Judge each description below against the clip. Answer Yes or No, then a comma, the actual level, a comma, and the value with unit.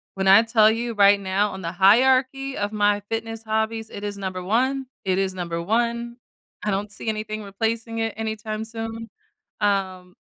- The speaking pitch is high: Yes, high, 215 Hz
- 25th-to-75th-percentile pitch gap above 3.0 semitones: No, narrow, 2.4 semitones